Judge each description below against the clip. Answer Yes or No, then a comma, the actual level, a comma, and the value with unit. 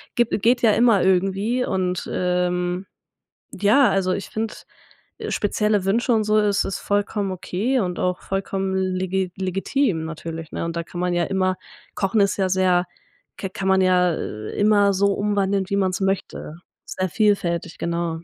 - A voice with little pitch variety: Yes, narrow, 2.2 semitones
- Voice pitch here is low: No, high, 190 Hz